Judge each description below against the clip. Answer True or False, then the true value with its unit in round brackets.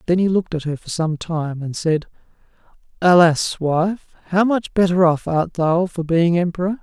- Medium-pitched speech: True (170 Hz)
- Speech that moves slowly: False (185 wpm)